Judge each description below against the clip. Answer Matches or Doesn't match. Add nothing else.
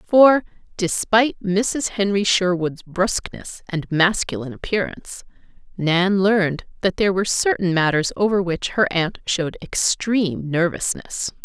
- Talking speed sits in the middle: Doesn't match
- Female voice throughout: Matches